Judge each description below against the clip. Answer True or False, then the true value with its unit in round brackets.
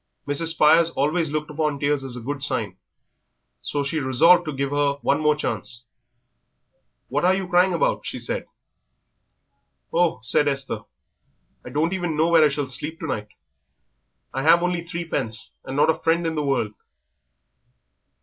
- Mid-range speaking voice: True (150 Hz)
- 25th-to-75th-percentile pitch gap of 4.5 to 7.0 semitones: False (3.1 semitones)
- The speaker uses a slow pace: False (160 wpm)